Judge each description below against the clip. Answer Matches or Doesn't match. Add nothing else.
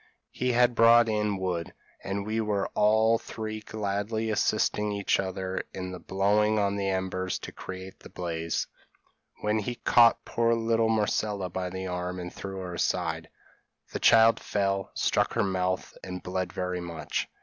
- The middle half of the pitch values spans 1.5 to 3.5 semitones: Matches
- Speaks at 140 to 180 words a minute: Matches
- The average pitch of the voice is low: Matches